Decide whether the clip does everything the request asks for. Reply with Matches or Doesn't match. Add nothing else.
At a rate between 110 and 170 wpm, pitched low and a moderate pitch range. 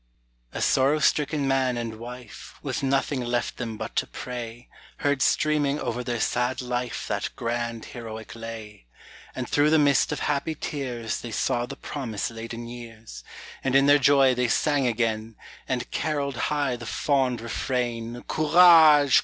Matches